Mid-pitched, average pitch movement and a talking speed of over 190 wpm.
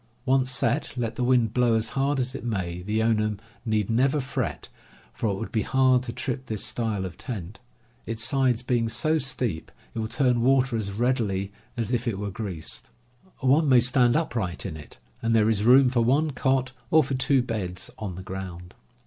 No: low, 115 Hz; average, 3.6 semitones; average, 200 wpm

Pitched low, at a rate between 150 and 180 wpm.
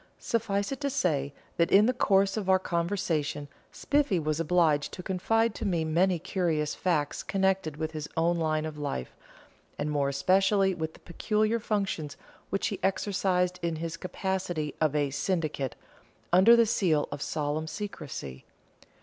No: medium, 175 Hz; average, 160 wpm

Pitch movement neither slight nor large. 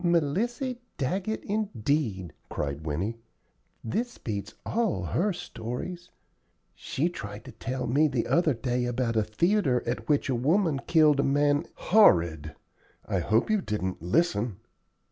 No: wide, 8.0 semitones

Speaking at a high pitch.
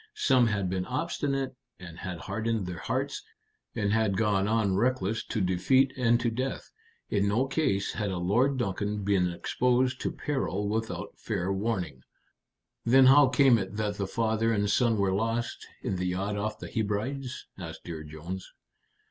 No: low, 105 Hz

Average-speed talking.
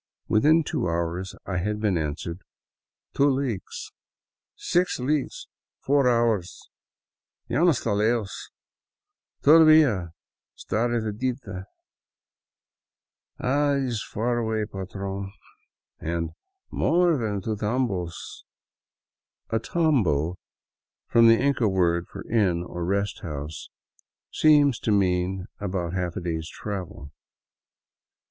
No: slow, 125 wpm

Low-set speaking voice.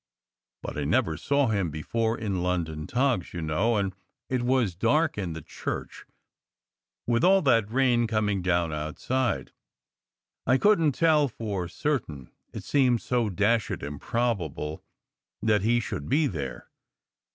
Yes: low, 110 Hz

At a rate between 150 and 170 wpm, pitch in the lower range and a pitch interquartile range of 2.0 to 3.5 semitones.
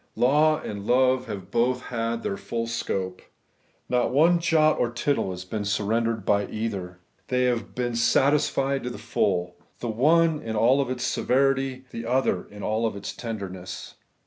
No: average, 160 wpm; low, 115 Hz; average, 4.1 semitones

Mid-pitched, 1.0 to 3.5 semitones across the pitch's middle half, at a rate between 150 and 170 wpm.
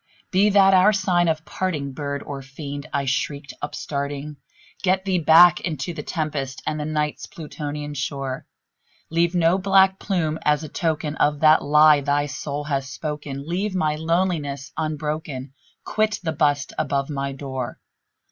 Yes: medium, 150 Hz; average, 3.2 semitones; average, 155 wpm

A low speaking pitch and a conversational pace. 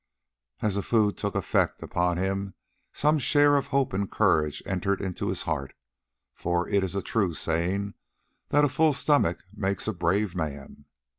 Yes: low, 100 Hz; average, 165 wpm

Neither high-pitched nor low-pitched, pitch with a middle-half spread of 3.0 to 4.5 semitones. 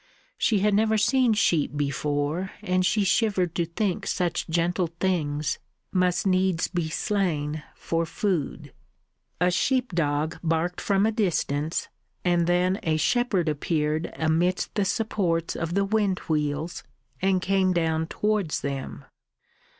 Yes: medium, 175 Hz; average, 3.7 semitones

